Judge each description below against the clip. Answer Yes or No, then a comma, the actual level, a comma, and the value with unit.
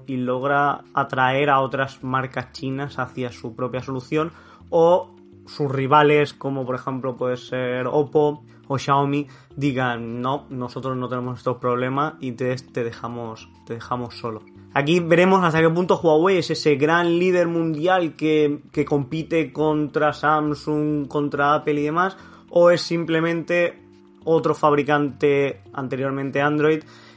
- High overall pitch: No, medium, 140 Hz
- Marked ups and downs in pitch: No, average, 3.4 semitones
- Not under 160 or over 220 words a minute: No, average, 135 wpm